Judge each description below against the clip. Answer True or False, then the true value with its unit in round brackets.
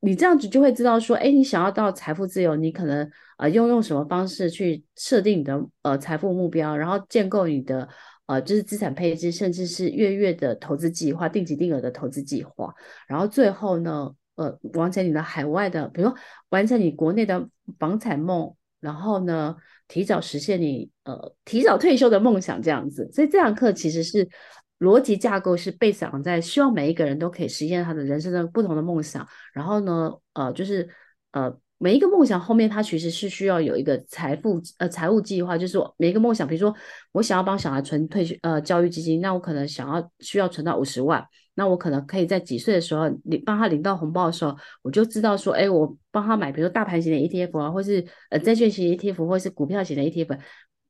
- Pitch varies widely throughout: False (4.6 semitones)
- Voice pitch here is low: False (175 Hz)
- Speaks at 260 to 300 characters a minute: False (330 characters per minute)